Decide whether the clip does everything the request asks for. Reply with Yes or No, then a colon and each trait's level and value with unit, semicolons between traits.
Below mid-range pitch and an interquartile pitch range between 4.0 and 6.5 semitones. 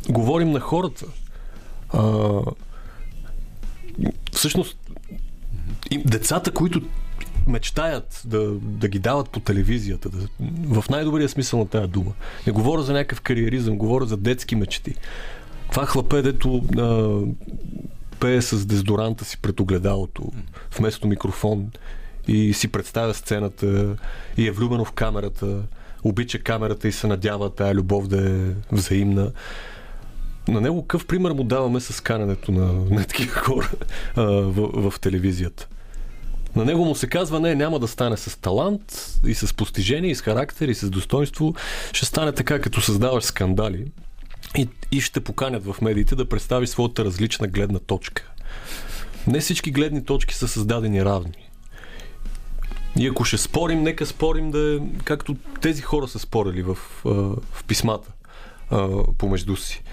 Yes: low, 110 Hz; average, 4.7 semitones